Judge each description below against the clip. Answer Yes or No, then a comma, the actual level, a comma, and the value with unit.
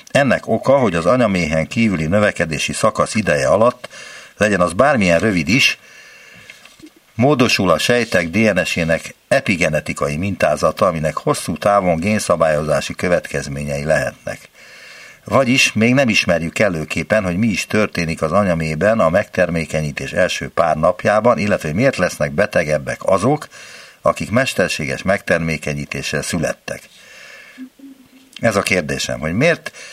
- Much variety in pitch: Yes, wide, 5.7 semitones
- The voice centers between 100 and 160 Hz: No, very low, 90 Hz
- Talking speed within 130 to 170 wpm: No, average, 115 wpm